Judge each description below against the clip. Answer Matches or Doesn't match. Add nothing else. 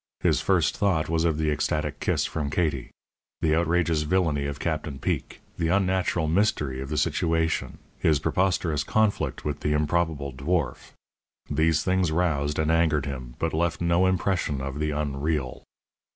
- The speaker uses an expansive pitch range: Doesn't match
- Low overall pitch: Matches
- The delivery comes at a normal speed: Matches